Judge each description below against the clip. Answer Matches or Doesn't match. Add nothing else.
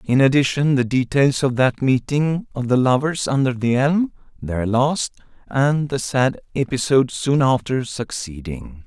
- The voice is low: Matches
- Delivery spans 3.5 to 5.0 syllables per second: Matches